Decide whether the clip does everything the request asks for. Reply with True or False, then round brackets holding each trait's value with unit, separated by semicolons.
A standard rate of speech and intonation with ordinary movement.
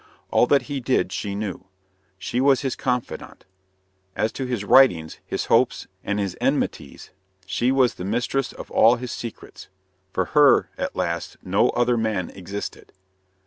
True (155 wpm; 4.3 semitones)